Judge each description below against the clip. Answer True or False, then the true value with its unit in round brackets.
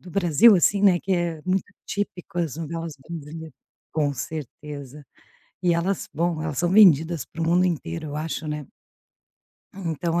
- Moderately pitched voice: True (165 Hz)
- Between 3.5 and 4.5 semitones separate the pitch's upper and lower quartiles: False (2.7 semitones)